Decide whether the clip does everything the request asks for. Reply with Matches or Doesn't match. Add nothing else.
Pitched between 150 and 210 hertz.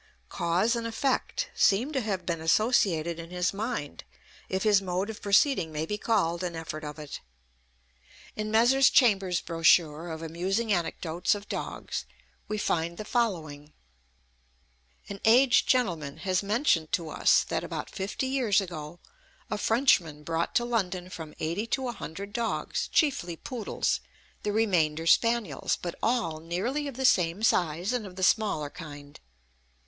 Matches